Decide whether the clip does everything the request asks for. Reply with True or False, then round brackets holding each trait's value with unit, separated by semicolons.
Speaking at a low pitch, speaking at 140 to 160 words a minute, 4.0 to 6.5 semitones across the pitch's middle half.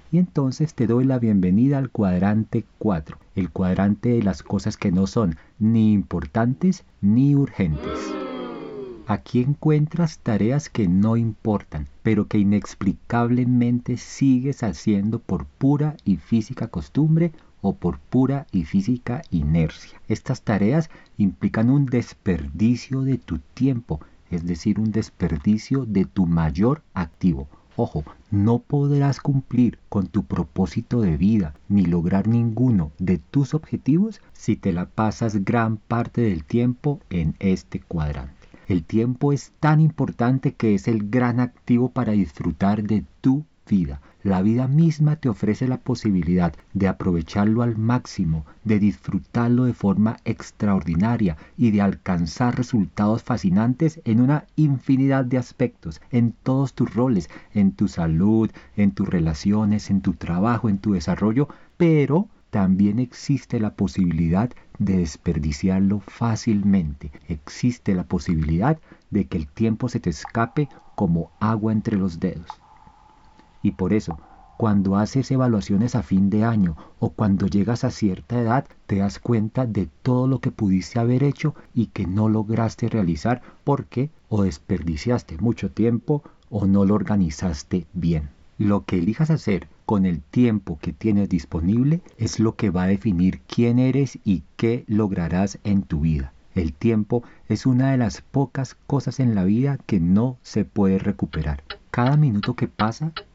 True (110 Hz; 145 wpm; 4.8 semitones)